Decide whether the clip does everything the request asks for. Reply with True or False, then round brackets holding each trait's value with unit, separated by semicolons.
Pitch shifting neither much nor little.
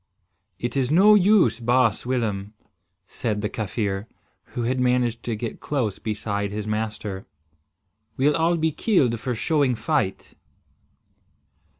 True (3.6 semitones)